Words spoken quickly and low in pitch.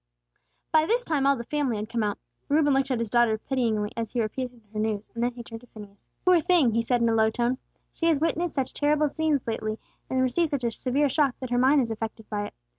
No: fast, 250 wpm; high, 245 Hz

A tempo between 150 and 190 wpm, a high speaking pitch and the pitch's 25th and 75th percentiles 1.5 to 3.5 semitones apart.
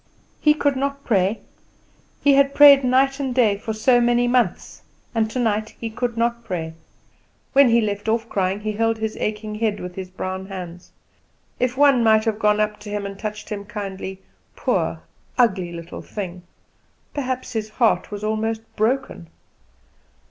Yes: average, 165 wpm; high, 220 Hz; average, 3.2 semitones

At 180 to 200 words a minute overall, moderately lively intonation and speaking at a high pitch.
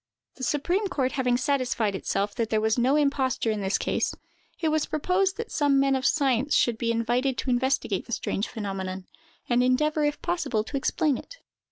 Yes: average, 190 wpm; average, 4.3 semitones; very high, 260 Hz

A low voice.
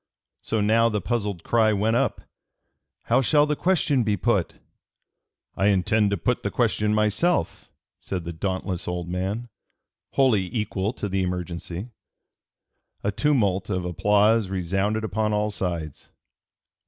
Yes: low, 105 Hz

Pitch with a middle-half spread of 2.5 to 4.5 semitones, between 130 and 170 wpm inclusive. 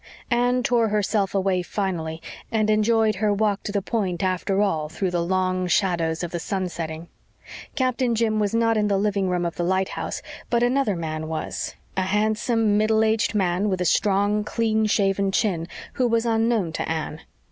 No: average, 3.5 semitones; average, 180 wpm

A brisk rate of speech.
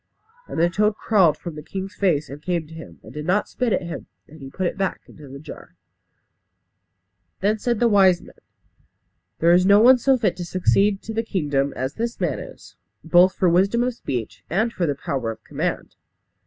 Yes: fast, 210 wpm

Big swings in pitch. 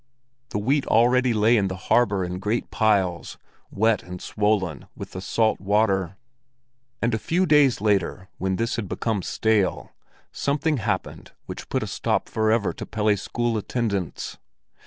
No: average, 3.4 semitones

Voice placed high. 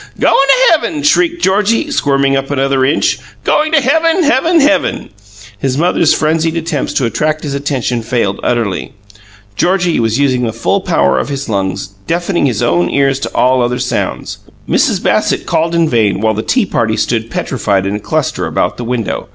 No: medium, 140 Hz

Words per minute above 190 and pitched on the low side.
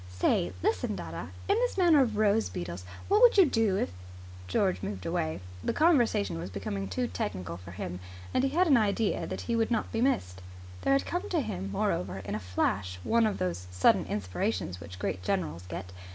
Yes: fast, 205 wpm; low, 100 Hz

